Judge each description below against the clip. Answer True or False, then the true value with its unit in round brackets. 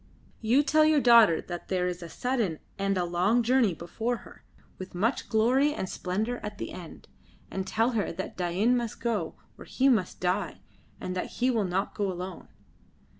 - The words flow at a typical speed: True (185 wpm)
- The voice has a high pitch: True (210 Hz)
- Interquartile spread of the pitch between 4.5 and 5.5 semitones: True (4.9 semitones)